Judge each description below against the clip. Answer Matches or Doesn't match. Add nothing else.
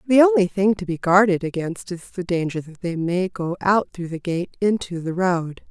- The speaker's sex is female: Matches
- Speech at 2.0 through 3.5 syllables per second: Doesn't match